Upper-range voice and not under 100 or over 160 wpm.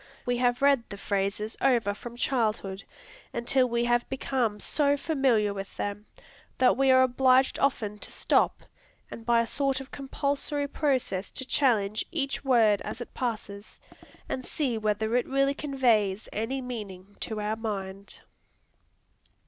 Yes: high, 240 Hz; average, 150 wpm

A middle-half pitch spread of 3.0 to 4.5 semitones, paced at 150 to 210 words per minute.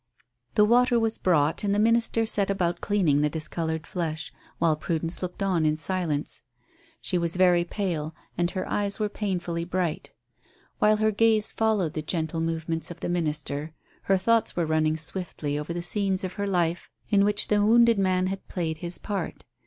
Yes: average, 4.0 semitones; average, 180 wpm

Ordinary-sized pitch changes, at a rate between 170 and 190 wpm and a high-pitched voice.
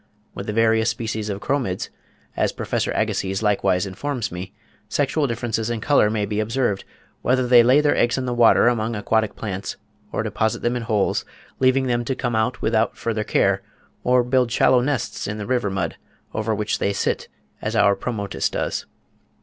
No: average, 3.0 semitones; average, 180 wpm; low, 115 Hz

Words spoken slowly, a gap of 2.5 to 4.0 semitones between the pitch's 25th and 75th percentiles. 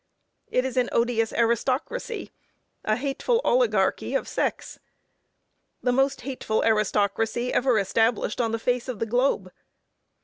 Yes: slow, 130 wpm; average, 2.8 semitones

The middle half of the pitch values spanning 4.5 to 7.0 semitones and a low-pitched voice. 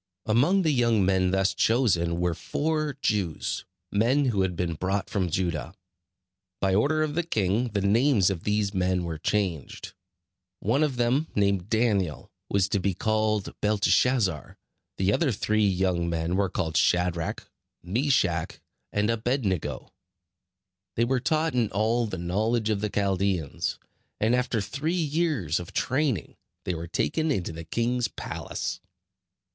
Yes: average, 5.1 semitones; low, 105 Hz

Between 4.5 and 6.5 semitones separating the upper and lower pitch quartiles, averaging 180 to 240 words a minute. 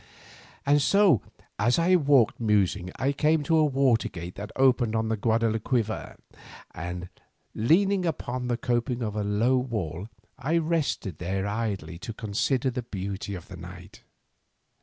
No: average, 5.2 semitones; average, 155 wpm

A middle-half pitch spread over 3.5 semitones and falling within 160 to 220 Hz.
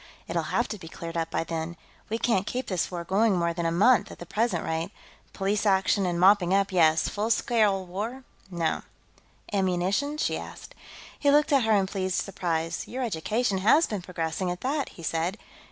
Yes: average, 4.2 semitones; high, 190 Hz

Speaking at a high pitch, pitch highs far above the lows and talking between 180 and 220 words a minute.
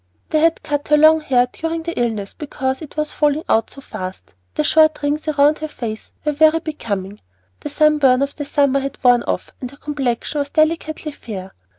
No: very high, 290 Hz; average, 3.7 semitones; average, 200 wpm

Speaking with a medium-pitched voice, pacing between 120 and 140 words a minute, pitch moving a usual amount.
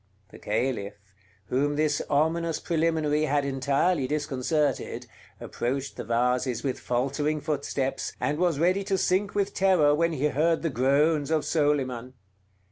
Yes: medium, 145 Hz; slow, 135 wpm; average, 3.4 semitones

